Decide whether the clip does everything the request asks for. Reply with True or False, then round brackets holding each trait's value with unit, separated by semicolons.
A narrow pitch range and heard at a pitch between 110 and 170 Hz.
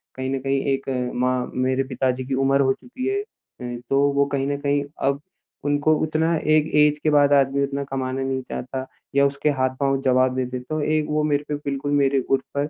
True (1.6 semitones; 140 Hz)